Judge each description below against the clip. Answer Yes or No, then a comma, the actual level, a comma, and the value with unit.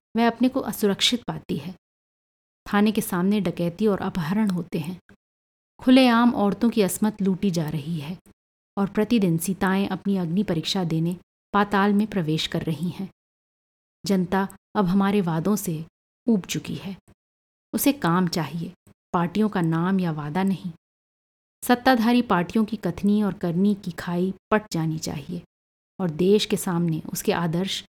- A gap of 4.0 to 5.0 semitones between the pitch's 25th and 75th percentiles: No, average, 3.2 semitones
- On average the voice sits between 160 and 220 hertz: Yes, high, 190 Hz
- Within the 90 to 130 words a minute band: No, average, 150 wpm